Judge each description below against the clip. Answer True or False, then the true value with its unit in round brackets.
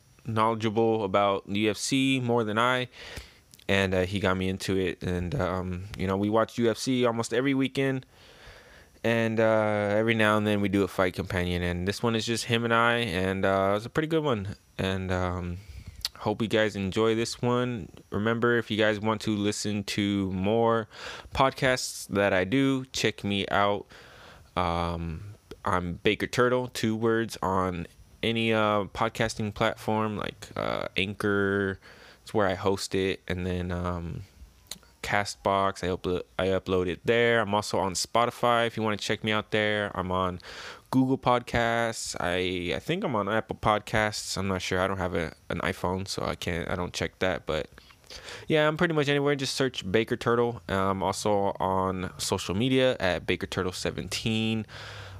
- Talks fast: False (175 wpm)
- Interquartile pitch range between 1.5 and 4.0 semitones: True (3.6 semitones)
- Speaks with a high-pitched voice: False (105 Hz)